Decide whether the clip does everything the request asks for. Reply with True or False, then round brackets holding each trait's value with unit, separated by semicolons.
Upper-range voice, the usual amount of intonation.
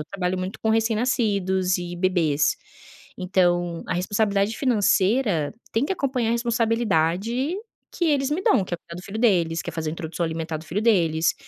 True (195 Hz; 4.9 semitones)